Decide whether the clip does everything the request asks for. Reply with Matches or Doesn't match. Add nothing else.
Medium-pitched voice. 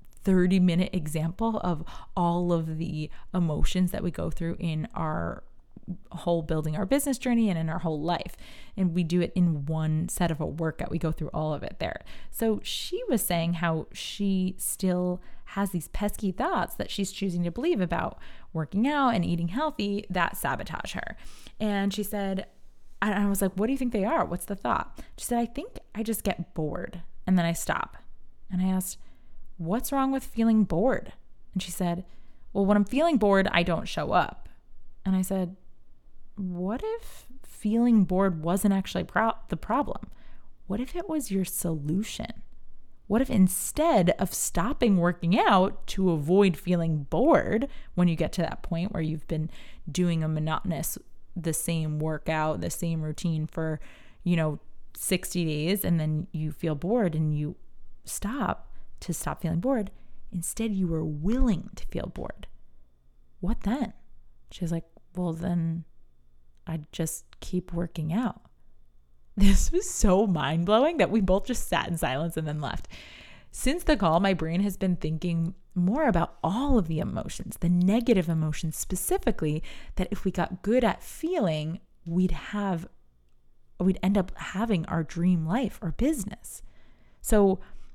Matches